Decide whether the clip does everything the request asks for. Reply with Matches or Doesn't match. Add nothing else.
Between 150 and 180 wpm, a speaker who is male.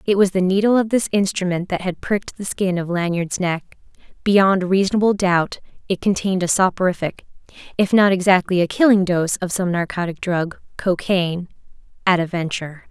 Doesn't match